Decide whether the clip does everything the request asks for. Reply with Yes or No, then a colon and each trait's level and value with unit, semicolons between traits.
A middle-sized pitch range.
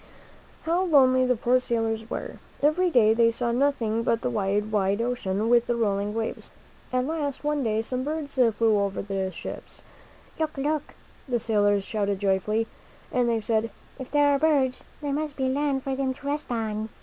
Yes: average, 4.4 semitones